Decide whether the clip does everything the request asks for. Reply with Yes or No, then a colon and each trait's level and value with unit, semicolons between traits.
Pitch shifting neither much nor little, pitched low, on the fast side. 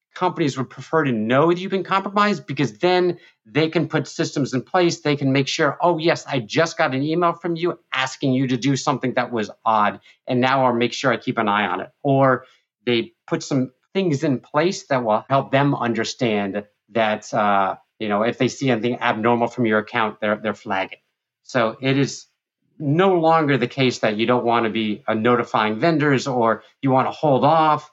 Yes: average, 5.0 semitones; low, 130 Hz; fast, 210 wpm